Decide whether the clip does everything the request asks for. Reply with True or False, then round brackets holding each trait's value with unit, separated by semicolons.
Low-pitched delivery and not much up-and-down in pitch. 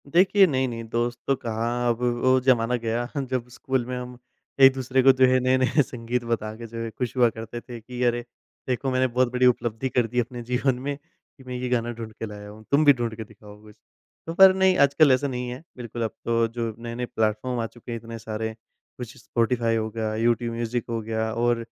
True (120 Hz; 2.0 semitones)